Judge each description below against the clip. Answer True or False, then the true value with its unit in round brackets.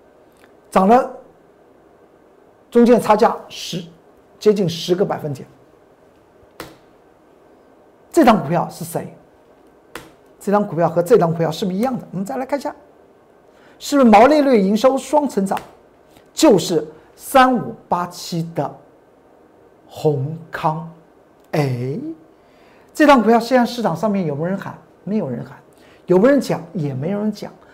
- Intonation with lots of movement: True (6.6 semitones)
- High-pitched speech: True (195 Hz)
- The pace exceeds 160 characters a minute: True (200 characters per minute)